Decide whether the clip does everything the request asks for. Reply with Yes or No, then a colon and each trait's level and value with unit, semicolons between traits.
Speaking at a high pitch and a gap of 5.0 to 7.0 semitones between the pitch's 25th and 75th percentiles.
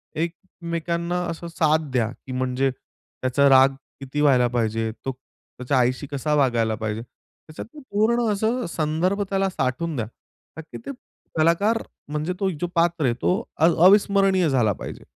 No: medium, 155 Hz; wide, 5.6 semitones